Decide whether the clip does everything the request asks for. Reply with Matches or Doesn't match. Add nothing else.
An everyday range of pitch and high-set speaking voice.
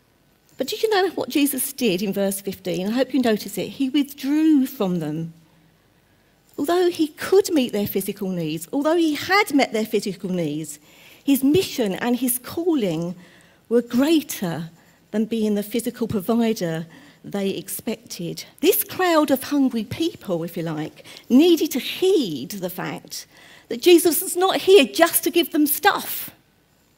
Doesn't match